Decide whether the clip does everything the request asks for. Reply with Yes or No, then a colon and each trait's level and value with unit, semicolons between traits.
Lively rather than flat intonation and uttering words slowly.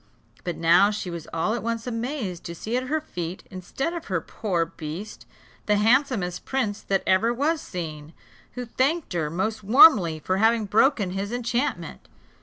No: wide, 5.7 semitones; average, 170 wpm